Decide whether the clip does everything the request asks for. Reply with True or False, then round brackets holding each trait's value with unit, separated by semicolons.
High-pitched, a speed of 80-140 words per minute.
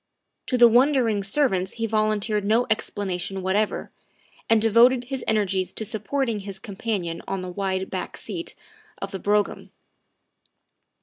True (210 Hz; 135 wpm)